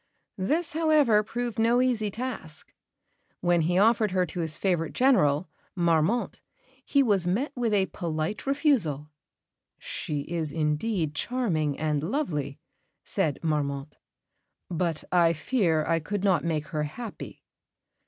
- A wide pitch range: Yes, wide, 6.8 semitones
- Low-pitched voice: No, medium, 180 Hz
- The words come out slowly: Yes, slow, 130 wpm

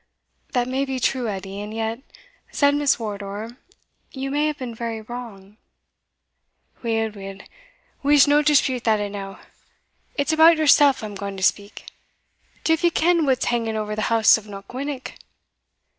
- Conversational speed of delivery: Yes, average, 150 wpm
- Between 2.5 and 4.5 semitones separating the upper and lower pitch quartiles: No, average, 5.2 semitones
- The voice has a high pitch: Yes, high, 235 Hz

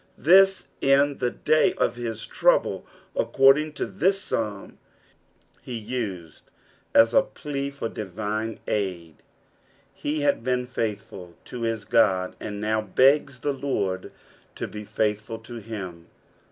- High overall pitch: No, low, 115 Hz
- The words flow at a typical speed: No, slow, 130 wpm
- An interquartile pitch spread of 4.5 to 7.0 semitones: Yes, average, 4.9 semitones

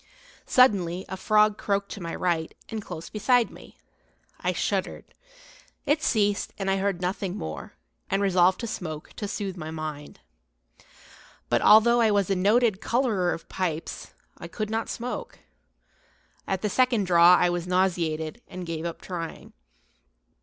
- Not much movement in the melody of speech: No, average, 3.6 semitones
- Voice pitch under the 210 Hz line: Yes, high, 190 Hz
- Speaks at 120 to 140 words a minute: No, average, 155 wpm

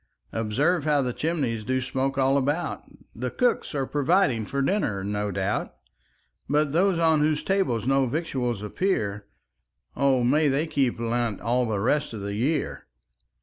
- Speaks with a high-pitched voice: No, low, 135 Hz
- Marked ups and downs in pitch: No, average, 4.7 semitones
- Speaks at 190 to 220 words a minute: No, average, 155 wpm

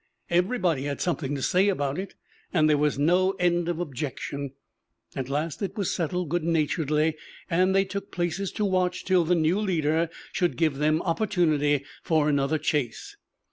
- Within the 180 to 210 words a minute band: No, average, 170 wpm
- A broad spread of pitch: No, average, 3.4 semitones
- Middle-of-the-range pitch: Yes, medium, 165 Hz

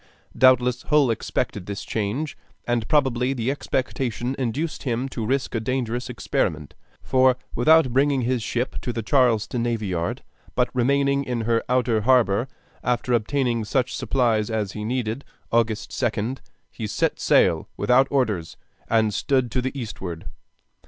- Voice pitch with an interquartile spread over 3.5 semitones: No, average, 2.8 semitones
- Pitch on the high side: No, low, 120 Hz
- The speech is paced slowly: No, average, 145 wpm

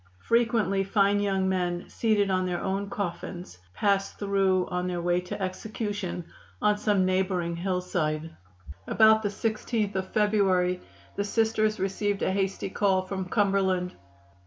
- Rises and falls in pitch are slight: Yes, narrow, 2.1 semitones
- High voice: Yes, high, 195 Hz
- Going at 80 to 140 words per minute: Yes, slow, 135 wpm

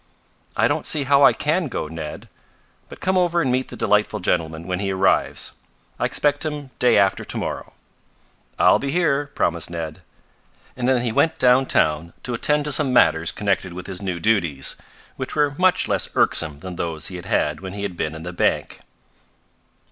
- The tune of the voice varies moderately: No, wide, 8.5 semitones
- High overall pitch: No, low, 100 Hz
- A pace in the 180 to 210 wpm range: Yes, average, 190 wpm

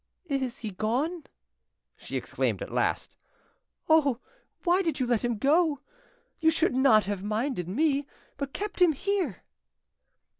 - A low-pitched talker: No, very high, 275 Hz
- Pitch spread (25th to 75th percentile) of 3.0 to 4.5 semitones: No, wide, 5.5 semitones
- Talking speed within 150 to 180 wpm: No, average, 140 wpm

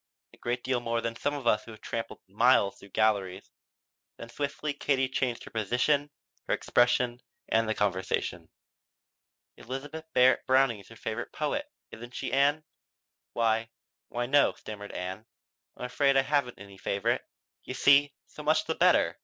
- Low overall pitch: Yes, low, 120 Hz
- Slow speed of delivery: No, average, 160 wpm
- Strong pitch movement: No, average, 3.9 semitones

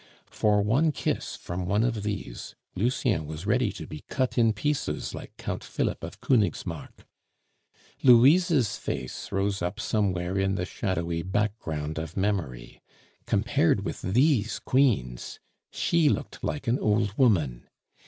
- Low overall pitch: Yes, low, 105 Hz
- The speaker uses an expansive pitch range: Yes, wide, 5.7 semitones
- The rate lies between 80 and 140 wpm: Yes, slow, 135 wpm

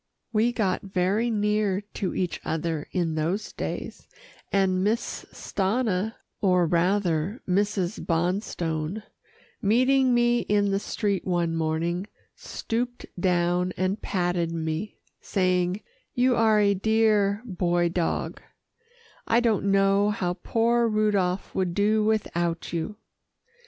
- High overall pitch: Yes, high, 195 Hz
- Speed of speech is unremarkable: No, slow, 115 wpm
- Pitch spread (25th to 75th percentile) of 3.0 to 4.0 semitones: Yes, average, 3.4 semitones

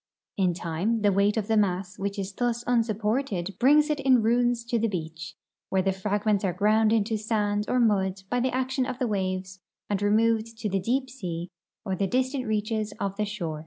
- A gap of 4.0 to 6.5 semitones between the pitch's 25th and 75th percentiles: No, average, 3.4 semitones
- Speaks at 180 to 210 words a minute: Yes, average, 200 wpm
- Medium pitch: No, high, 210 Hz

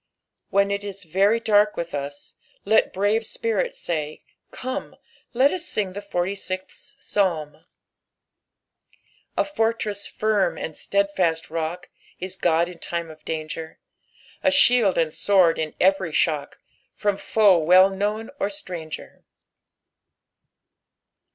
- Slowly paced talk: Yes, slow, 125 wpm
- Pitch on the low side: No, high, 190 Hz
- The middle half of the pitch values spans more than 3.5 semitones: Yes, average, 3.9 semitones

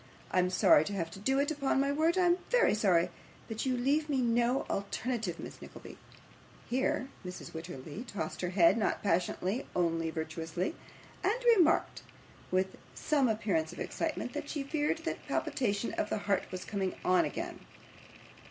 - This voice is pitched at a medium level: No, high, 210 Hz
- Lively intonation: Yes, wide, 7.1 semitones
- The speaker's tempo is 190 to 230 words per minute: No, average, 170 wpm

